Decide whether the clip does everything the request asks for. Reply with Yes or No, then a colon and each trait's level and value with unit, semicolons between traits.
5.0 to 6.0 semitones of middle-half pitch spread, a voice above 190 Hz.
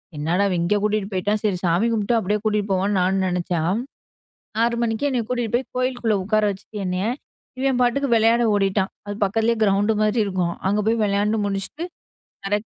No: average, 2.9 semitones; high, 210 Hz